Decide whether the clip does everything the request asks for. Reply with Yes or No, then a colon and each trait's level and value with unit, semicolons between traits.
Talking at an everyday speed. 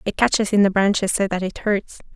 No: fast, 250 wpm